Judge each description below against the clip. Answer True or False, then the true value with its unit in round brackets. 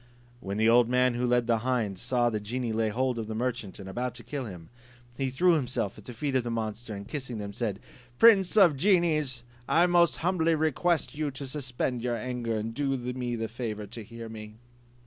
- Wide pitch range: False (3.5 semitones)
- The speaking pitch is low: True (120 Hz)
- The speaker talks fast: True (225 wpm)